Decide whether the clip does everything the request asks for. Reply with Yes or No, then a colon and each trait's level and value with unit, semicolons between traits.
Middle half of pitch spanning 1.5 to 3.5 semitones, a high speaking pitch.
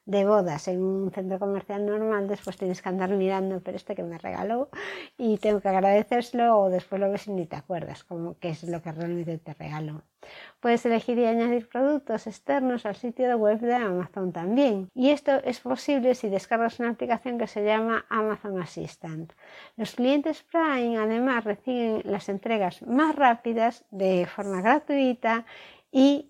No: average, 4.2 semitones; high, 215 Hz